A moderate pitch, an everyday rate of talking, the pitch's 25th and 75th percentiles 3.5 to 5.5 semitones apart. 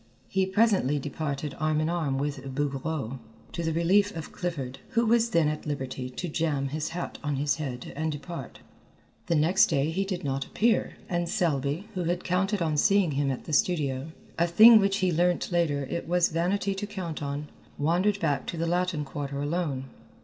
Yes: medium, 160 Hz; average, 190 wpm; average, 4.0 semitones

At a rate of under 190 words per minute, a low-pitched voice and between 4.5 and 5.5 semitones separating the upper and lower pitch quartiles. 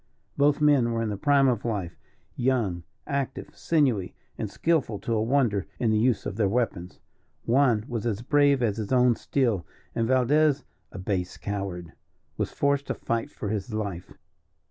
Yes: average, 170 wpm; low, 115 Hz; average, 4.9 semitones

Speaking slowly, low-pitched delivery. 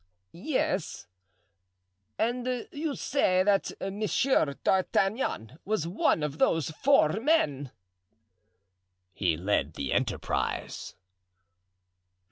No: slow, 85 wpm; high, 190 Hz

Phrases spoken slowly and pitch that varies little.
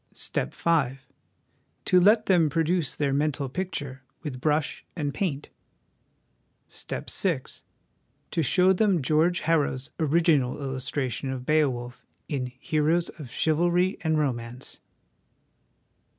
No: slow, 120 wpm; average, 4.2 semitones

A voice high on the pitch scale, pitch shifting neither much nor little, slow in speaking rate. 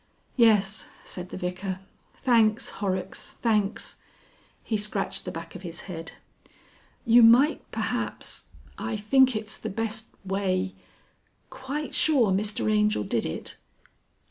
Yes: high, 210 Hz; average, 3.3 semitones; slow, 120 wpm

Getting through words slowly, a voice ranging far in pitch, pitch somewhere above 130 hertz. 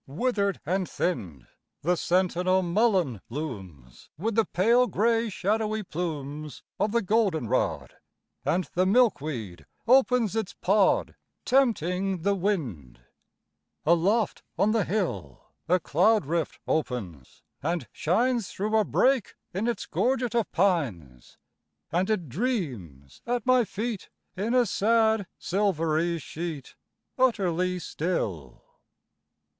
Yes: slow, 110 wpm; wide, 6.2 semitones; medium, 185 Hz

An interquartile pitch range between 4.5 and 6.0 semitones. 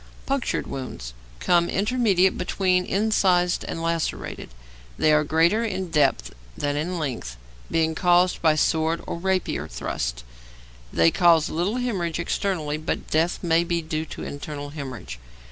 No: average, 3.3 semitones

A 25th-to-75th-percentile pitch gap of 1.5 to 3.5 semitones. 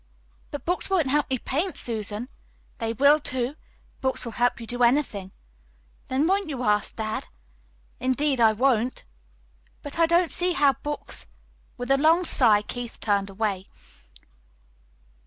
No: average, 4.7 semitones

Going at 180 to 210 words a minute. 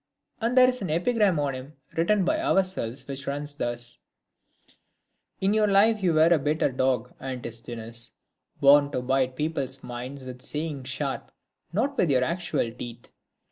No: average, 155 wpm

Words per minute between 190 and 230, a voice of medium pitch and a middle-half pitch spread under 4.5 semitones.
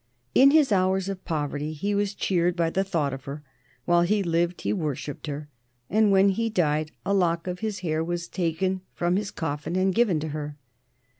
Yes: average, 200 wpm; medium, 175 Hz; average, 3.9 semitones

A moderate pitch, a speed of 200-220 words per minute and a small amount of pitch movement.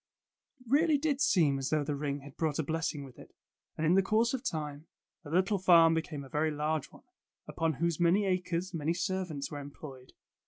No: medium, 160 Hz; fast, 205 wpm; average, 4.2 semitones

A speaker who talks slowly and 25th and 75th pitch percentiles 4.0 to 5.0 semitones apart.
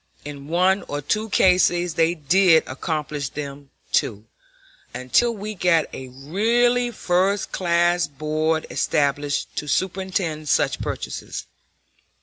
Yes: slow, 115 wpm; average, 4.5 semitones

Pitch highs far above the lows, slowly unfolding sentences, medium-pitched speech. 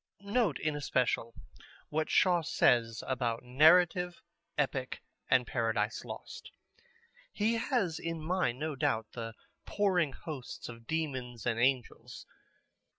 Yes: wide, 5.8 semitones; slow, 115 wpm; medium, 145 Hz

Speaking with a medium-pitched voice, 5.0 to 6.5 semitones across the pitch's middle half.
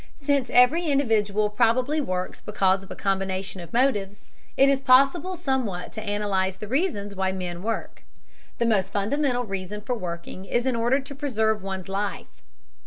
No: high, 215 Hz; average, 5.3 semitones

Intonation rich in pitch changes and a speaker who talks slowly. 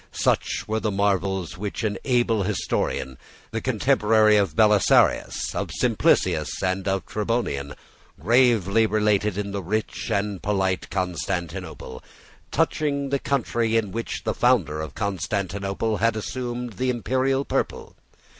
No: average, 3.2 semitones; slow, 125 wpm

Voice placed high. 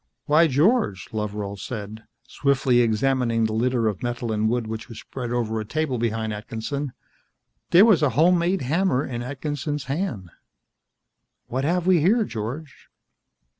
No: low, 125 Hz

